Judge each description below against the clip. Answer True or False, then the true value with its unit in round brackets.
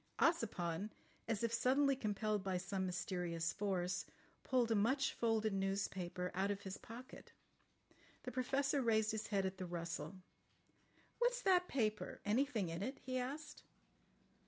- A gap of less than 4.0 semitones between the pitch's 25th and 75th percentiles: False (5.3 semitones)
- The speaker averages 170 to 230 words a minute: False (140 wpm)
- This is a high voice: True (215 Hz)